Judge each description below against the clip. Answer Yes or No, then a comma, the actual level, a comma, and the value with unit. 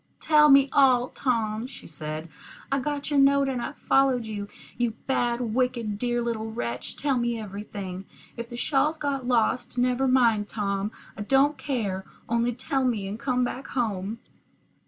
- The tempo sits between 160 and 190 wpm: Yes, average, 165 wpm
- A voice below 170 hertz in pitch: No, high, 240 Hz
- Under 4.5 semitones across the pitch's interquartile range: Yes, average, 3.9 semitones